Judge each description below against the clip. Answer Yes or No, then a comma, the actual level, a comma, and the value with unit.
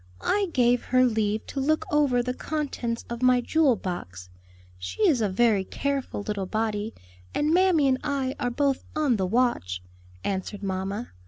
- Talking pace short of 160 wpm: No, average, 165 wpm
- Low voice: No, high, 240 Hz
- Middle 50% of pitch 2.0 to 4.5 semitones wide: No, average, 5.2 semitones